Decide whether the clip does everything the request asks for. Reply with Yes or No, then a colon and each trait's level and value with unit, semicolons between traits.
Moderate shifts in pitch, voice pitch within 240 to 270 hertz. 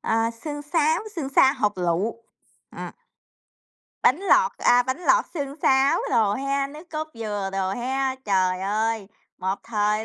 No: wide, 5.7 semitones; high, 245 Hz